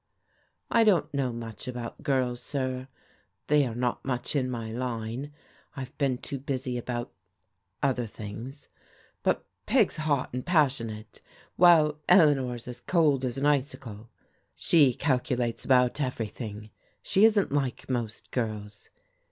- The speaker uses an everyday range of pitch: Yes, average, 3.3 semitones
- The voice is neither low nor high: No, low, 130 Hz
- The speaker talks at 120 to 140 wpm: Yes, slow, 135 wpm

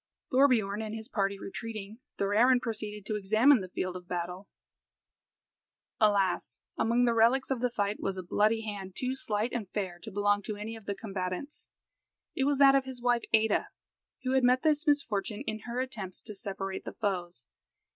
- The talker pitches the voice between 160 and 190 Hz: No, high, 215 Hz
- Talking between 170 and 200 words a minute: Yes, average, 180 wpm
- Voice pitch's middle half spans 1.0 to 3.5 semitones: No, average, 3.9 semitones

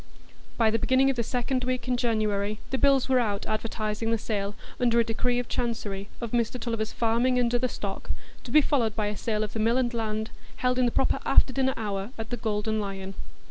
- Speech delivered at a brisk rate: Yes, fast, 220 wpm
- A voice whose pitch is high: Yes, high, 230 Hz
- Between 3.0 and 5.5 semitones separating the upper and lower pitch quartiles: No, narrow, 2.6 semitones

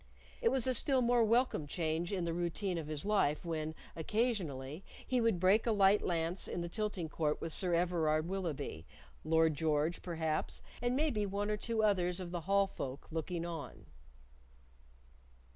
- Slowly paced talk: No, average, 170 wpm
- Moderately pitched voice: Yes, medium, 175 Hz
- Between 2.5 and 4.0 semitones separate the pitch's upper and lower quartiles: No, average, 4.7 semitones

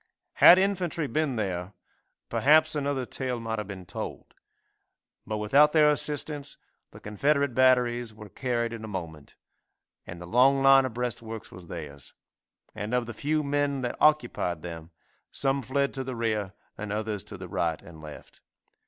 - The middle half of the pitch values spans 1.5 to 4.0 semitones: No, average, 5.3 semitones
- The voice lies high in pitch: No, low, 120 Hz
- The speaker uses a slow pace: No, average, 160 wpm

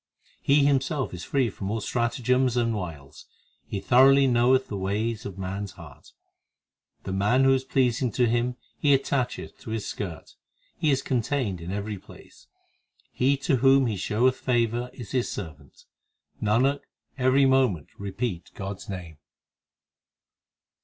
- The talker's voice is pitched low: Yes, low, 120 Hz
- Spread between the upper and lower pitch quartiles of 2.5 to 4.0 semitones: No, average, 4.8 semitones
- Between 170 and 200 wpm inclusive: No, average, 150 wpm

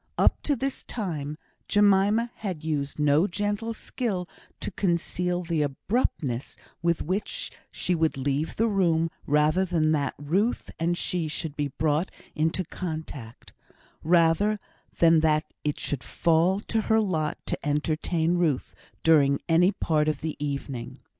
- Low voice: No, medium, 165 Hz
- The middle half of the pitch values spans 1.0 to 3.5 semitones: No, average, 3.9 semitones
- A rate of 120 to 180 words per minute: Yes, average, 140 wpm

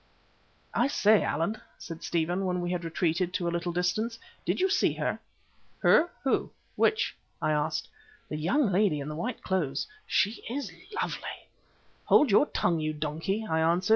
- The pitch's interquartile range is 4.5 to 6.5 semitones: Yes, average, 5.0 semitones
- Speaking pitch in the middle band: Yes, medium, 180 Hz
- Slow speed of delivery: No, average, 170 wpm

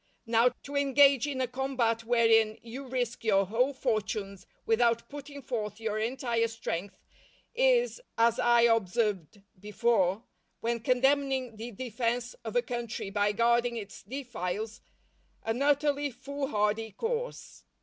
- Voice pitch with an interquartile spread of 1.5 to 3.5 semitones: Yes, average, 3.2 semitones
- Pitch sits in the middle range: No, high, 235 Hz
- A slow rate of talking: Yes, slow, 130 wpm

